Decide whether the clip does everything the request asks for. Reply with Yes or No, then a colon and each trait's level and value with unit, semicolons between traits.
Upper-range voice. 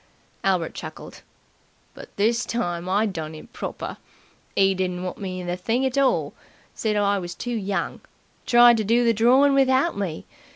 Yes: high, 205 Hz